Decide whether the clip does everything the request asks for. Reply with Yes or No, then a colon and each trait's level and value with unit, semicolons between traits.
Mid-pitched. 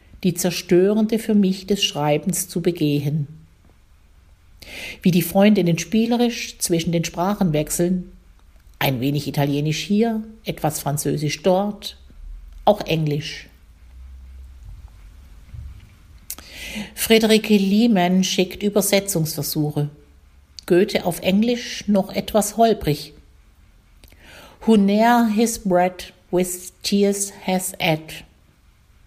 Yes: medium, 165 Hz